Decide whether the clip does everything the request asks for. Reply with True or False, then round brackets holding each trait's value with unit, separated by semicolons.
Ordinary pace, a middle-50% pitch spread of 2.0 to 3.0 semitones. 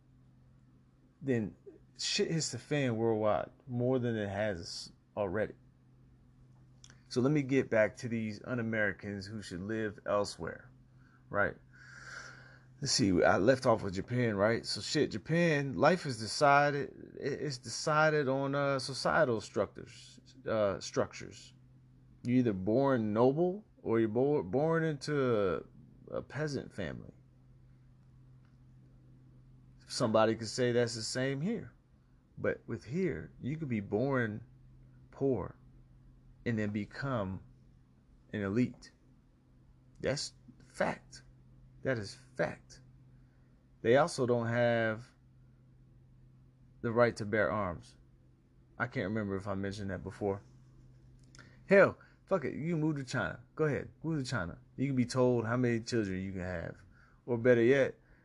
False (130 wpm; 2.5 semitones)